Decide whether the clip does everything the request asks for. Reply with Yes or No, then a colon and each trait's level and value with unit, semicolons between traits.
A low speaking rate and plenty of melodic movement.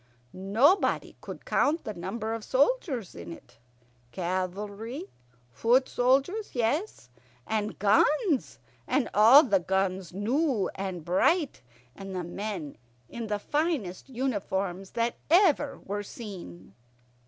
Yes: slow, 115 wpm; wide, 6.1 semitones